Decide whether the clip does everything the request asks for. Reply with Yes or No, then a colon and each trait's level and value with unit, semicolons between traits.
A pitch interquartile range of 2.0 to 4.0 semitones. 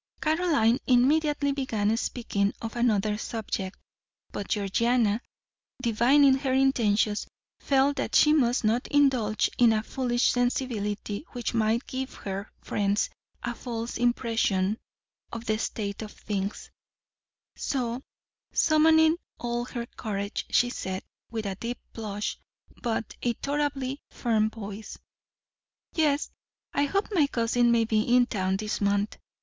Yes: average, 3.7 semitones